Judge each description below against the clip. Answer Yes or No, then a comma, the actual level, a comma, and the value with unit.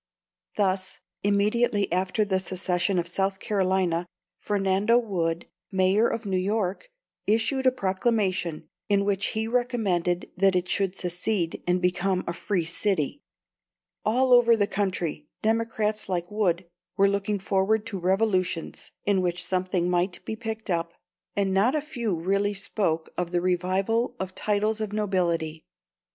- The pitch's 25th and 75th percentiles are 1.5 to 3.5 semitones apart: Yes, average, 3.0 semitones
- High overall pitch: Yes, high, 195 Hz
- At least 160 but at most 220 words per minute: No, average, 140 wpm